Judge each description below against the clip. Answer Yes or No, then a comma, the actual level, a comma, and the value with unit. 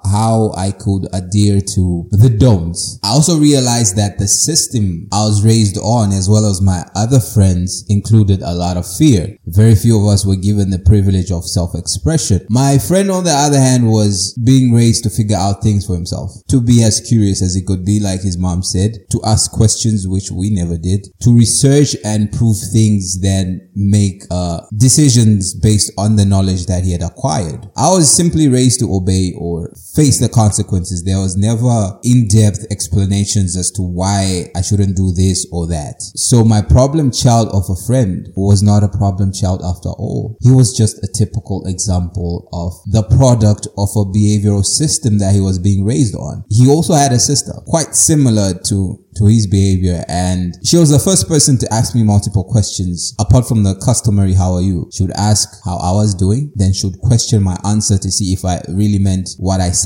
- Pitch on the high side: No, low, 105 Hz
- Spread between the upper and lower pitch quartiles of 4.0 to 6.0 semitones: No, average, 3.4 semitones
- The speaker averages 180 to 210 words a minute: Yes, average, 195 wpm